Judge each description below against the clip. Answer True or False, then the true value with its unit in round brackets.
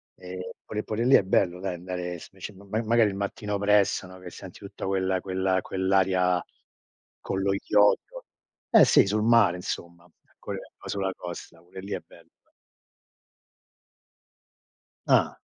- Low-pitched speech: True (95 Hz)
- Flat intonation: True (1.9 semitones)